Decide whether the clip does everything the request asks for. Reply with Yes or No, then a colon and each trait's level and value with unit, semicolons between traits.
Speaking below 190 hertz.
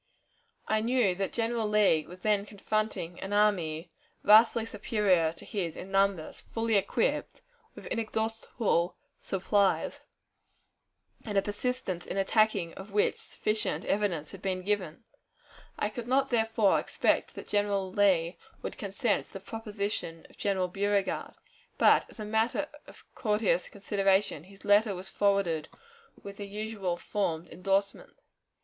No: high, 200 Hz